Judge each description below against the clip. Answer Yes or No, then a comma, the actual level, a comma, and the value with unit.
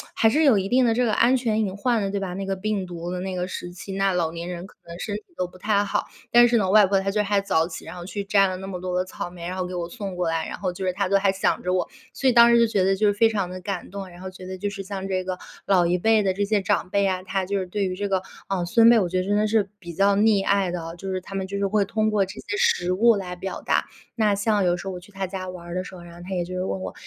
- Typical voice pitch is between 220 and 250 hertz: No, high, 195 Hz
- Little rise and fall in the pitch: Yes, narrow, 2.1 semitones